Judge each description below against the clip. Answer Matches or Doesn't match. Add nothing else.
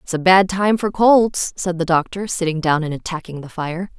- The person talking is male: Doesn't match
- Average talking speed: Doesn't match